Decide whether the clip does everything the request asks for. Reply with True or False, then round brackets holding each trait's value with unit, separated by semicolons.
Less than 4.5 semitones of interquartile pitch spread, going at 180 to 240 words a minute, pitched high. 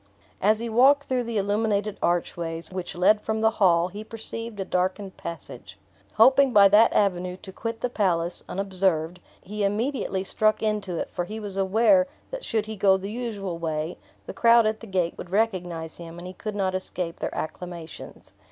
True (3.5 semitones; 185 wpm; 200 Hz)